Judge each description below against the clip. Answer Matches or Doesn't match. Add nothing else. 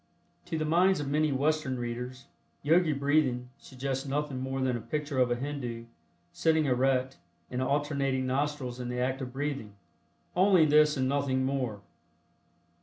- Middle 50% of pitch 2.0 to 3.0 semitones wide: Matches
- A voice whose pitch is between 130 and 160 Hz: Matches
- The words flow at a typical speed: Matches